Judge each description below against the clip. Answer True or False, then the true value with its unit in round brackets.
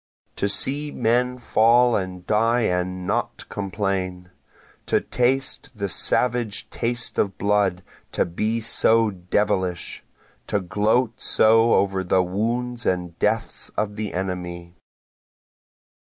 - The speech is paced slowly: True (115 wpm)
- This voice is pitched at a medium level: False (105 Hz)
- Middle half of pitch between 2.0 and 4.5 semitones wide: True (3.9 semitones)